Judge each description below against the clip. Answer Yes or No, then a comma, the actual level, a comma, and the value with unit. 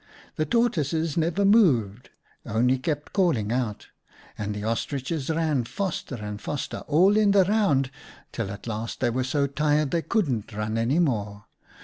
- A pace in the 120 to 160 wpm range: Yes, average, 155 wpm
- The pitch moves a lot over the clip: Yes, wide, 6.5 semitones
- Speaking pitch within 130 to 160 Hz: Yes, medium, 140 Hz